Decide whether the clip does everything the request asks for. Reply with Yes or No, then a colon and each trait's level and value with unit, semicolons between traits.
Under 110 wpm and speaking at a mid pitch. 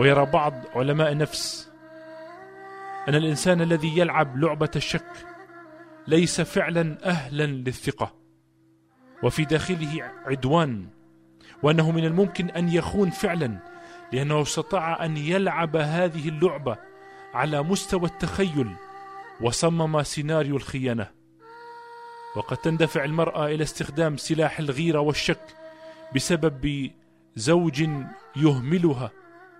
Yes: average, 95 wpm; medium, 160 Hz